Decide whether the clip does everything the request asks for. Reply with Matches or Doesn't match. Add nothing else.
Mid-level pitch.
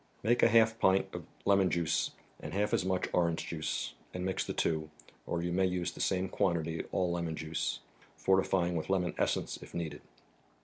Doesn't match